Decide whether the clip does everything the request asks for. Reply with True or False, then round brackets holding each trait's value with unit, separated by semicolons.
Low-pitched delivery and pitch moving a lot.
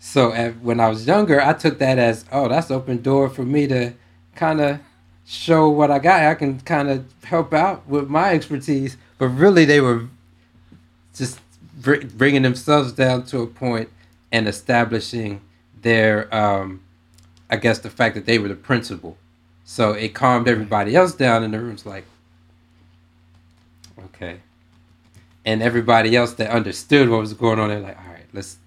True (115 Hz; 6.8 semitones)